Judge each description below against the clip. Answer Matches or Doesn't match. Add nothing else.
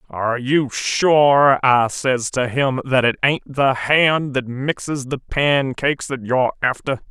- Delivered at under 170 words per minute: Matches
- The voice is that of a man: Matches